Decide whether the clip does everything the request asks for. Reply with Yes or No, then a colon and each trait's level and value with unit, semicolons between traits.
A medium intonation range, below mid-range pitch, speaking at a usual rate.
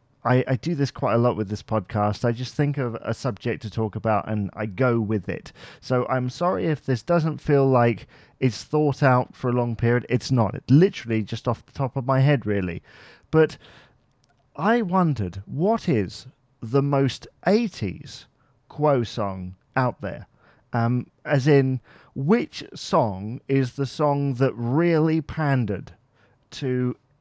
Yes: average, 3.7 semitones; low, 125 Hz; average, 165 wpm